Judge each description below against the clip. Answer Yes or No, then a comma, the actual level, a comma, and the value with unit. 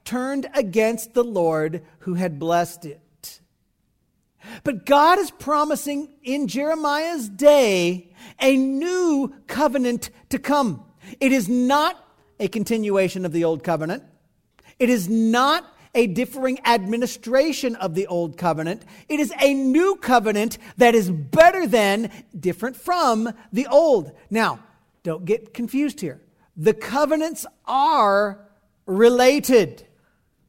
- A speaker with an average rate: No, slow, 120 wpm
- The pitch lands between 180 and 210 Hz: No, high, 235 Hz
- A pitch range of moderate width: No, wide, 6.0 semitones